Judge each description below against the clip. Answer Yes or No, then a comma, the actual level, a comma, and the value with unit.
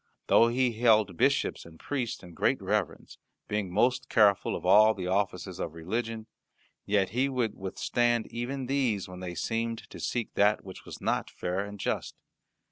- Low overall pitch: Yes, low, 110 Hz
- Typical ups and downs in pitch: Yes, average, 3.9 semitones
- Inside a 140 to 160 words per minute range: No, average, 170 wpm